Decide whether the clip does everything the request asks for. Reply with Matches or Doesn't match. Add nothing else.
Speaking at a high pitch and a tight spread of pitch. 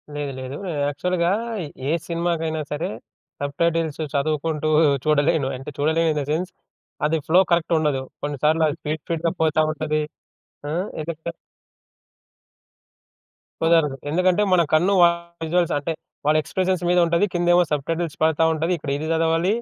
Doesn't match